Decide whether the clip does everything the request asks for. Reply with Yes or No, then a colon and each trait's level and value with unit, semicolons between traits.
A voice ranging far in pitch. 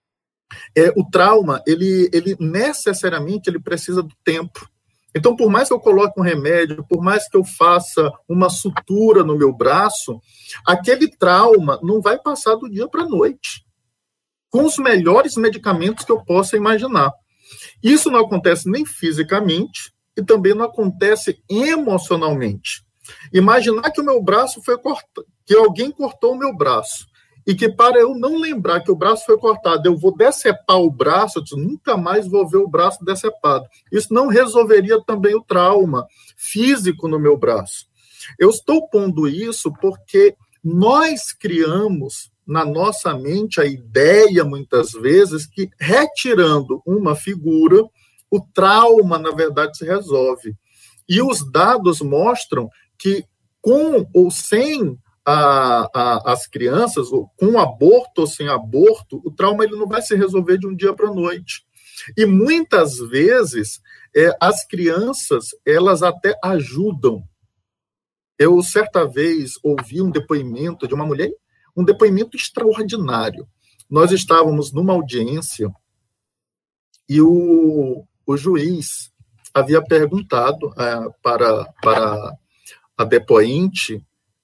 Yes: wide, 6.8 semitones